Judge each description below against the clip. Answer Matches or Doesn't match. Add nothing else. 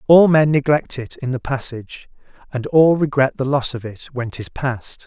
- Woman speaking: Doesn't match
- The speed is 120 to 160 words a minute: Doesn't match